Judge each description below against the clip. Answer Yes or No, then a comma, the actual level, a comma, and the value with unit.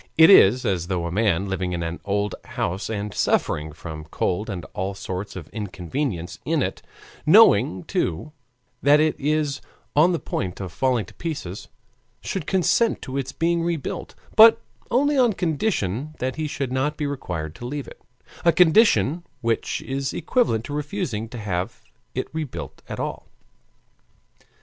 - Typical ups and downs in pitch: No, wide, 8.6 semitones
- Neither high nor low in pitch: No, low, 125 Hz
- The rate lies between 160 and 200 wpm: Yes, average, 165 wpm